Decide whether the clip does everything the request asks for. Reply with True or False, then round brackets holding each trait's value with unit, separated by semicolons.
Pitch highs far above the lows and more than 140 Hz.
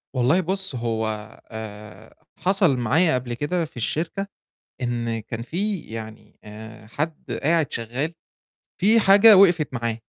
False (7.7 semitones; 130 Hz)